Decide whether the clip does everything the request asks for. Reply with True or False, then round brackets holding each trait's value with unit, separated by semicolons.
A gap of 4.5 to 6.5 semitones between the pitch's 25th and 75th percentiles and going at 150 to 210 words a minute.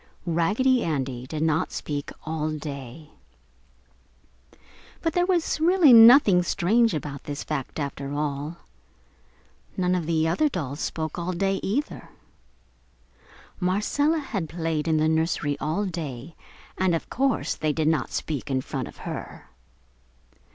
False (5.1 semitones; 135 wpm)